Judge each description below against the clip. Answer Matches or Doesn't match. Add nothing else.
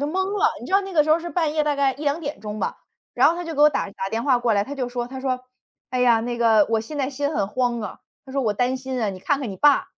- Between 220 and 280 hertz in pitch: Matches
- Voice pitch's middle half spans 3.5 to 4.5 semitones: Matches